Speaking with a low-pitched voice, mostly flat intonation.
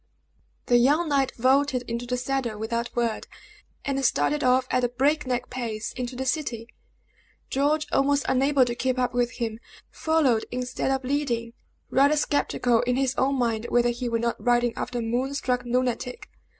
No: very high, 250 Hz; narrow, 2.1 semitones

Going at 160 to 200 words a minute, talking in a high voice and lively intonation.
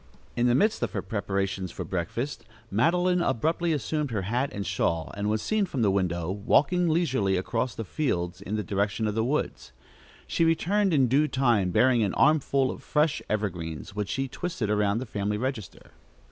No: average, 185 wpm; low, 115 Hz; wide, 6.9 semitones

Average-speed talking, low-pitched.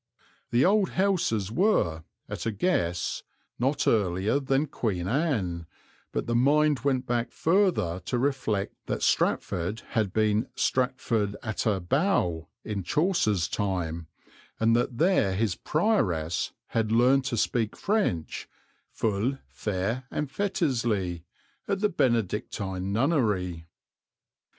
No: slow, 115 wpm; low, 115 Hz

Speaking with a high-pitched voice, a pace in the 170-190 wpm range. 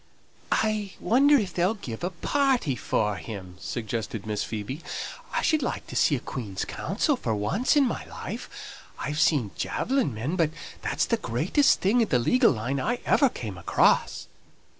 No: medium, 150 Hz; average, 175 wpm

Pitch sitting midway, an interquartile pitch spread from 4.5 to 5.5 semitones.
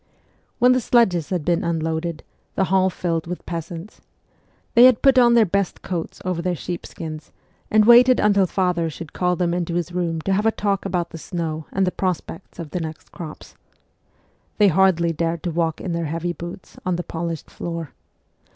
No: medium, 175 Hz; narrow, 2.5 semitones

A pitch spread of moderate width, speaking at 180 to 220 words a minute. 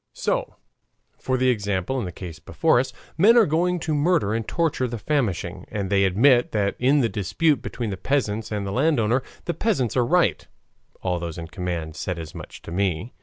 No: wide, 7.4 semitones; average, 195 wpm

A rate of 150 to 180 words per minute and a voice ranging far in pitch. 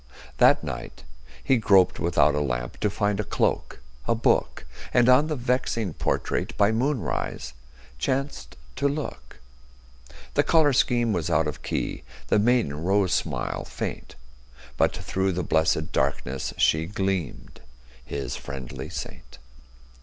No: slow, 135 wpm; wide, 8.4 semitones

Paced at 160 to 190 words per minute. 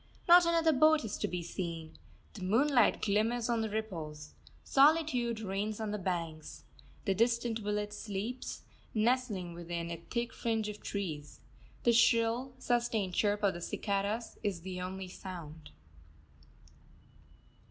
No: slow, 135 wpm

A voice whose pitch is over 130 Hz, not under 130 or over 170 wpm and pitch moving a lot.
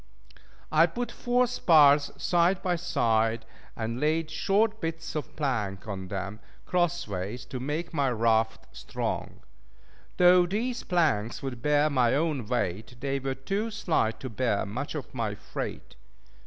Yes: medium, 140 Hz; average, 145 wpm; wide, 7.3 semitones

